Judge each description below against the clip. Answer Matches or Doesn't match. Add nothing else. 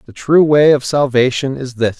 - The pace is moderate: Doesn't match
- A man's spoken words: Matches